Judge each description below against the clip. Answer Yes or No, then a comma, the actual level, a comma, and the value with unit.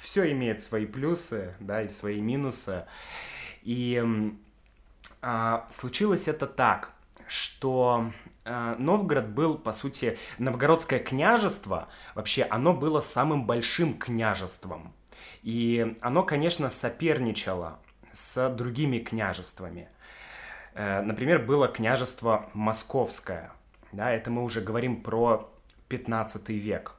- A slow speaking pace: Yes, slow, 105 wpm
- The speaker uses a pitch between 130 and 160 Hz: No, low, 120 Hz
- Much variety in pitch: No, average, 3.6 semitones